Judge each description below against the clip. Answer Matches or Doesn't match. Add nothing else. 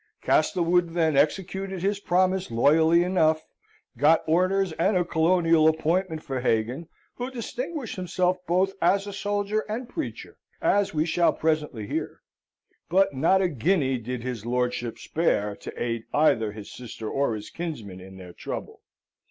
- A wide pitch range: Matches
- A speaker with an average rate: Matches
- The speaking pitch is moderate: Matches